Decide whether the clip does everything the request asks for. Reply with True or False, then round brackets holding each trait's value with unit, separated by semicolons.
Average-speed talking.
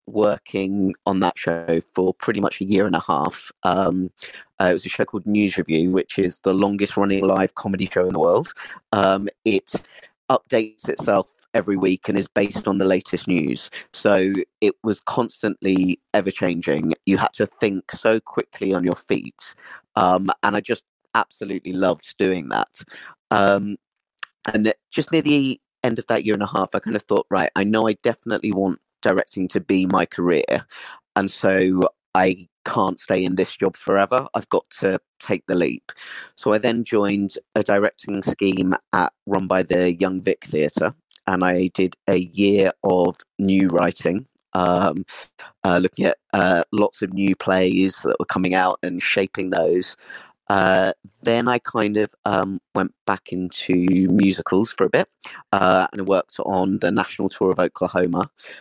True (175 wpm)